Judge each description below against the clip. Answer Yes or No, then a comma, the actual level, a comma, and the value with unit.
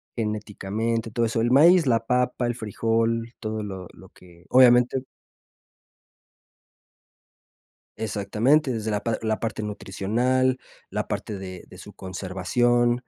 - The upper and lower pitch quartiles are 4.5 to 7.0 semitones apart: No, average, 2.9 semitones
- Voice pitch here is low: Yes, low, 115 Hz